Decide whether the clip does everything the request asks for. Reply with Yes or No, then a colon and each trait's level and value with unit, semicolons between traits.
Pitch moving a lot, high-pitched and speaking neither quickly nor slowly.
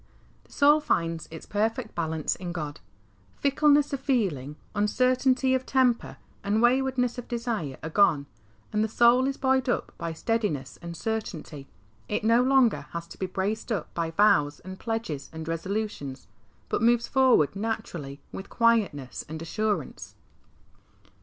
Yes: wide, 7.1 semitones; high, 215 Hz; average, 145 wpm